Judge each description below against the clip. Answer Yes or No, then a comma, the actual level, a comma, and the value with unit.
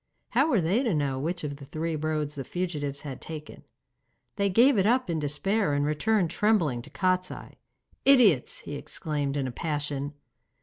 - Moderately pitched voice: Yes, medium, 155 Hz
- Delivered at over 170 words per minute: Yes, average, 180 wpm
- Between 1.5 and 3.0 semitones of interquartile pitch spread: No, wide, 5.4 semitones